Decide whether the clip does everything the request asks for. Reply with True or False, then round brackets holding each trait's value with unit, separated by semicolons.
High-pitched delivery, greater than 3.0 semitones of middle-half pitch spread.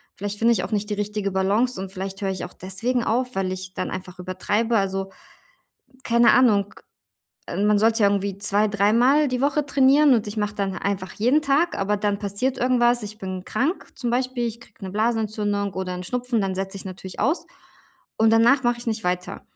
True (210 Hz; 3.7 semitones)